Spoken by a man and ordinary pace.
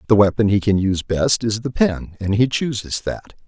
No: male; fast, 225 wpm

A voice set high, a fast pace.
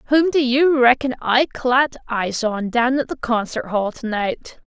No: very high, 250 Hz; average, 180 wpm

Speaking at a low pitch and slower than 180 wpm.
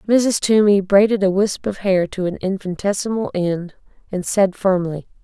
No: high, 195 Hz; average, 160 wpm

